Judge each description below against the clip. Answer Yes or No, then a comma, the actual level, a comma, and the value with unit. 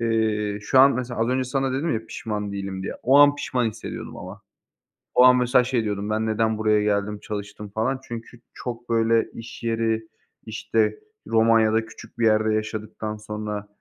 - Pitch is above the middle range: No, low, 110 Hz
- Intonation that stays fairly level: Yes, narrow, 2.1 semitones